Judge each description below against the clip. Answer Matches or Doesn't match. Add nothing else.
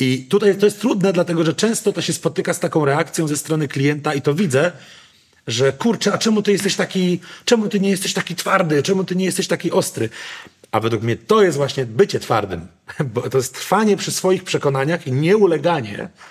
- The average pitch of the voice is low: Doesn't match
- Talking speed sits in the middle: Doesn't match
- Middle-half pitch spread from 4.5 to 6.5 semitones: Matches